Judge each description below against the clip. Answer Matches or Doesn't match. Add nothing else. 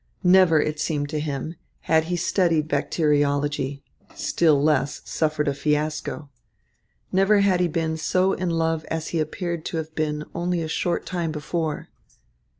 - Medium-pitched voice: Matches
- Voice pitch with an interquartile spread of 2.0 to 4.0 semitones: Matches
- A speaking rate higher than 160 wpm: Doesn't match